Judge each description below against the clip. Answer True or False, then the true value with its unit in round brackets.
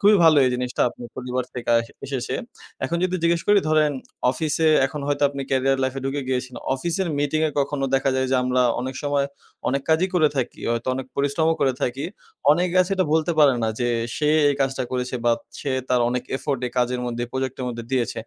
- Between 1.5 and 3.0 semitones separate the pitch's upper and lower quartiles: False (3.4 semitones)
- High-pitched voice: False (135 Hz)